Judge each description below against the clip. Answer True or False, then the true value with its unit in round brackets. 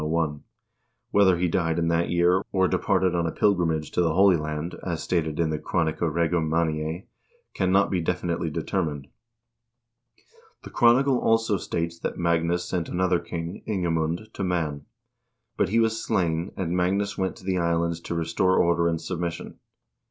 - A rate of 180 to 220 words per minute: False (160 wpm)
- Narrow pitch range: True (2.1 semitones)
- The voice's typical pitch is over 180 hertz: False (85 Hz)